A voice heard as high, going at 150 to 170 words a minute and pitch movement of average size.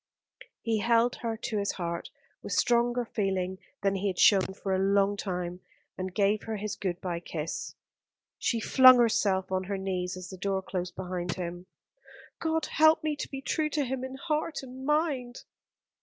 No: high, 200 Hz; average, 180 wpm; average, 5.0 semitones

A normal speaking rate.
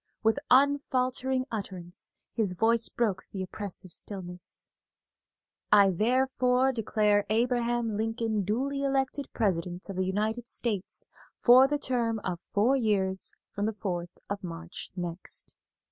No: slow, 125 wpm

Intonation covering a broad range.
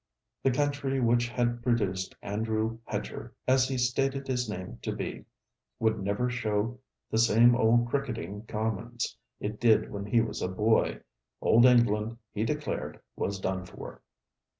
No: average, 2.7 semitones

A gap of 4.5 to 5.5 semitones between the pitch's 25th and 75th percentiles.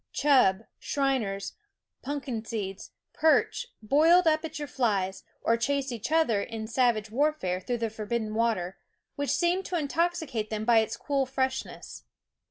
Yes: average, 5.2 semitones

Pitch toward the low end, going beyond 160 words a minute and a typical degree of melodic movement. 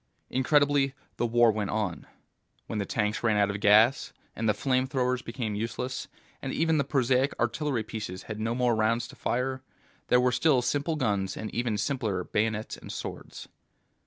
Yes: low, 120 Hz; average, 175 wpm; average, 3.4 semitones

